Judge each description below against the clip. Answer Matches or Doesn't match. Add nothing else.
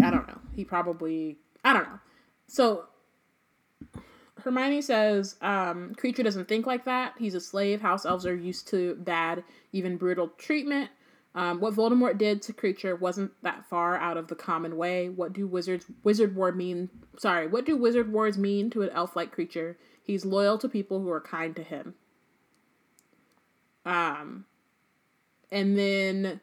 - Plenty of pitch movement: Doesn't match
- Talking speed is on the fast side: Doesn't match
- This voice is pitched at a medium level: Doesn't match